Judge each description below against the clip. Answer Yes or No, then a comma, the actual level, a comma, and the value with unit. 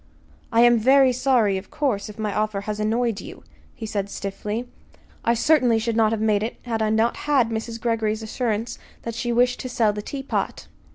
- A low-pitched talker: No, high, 225 Hz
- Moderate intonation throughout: No, narrow, 2.2 semitones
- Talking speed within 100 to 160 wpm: No, average, 195 wpm